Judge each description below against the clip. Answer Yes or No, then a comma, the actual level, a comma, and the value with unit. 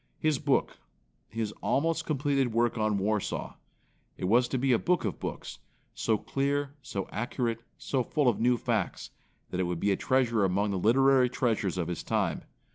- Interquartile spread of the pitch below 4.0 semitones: No, average, 4.6 semitones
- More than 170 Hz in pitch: No, low, 120 Hz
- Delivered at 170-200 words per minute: Yes, average, 185 wpm